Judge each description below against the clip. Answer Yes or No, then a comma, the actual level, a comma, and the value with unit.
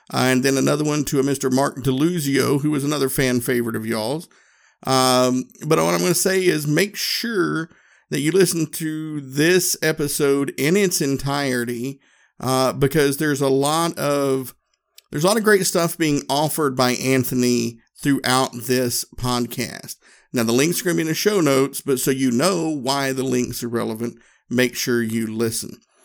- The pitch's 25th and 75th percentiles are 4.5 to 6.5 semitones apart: No, average, 3.7 semitones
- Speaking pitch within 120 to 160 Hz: Yes, medium, 140 Hz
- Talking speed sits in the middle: Yes, average, 180 wpm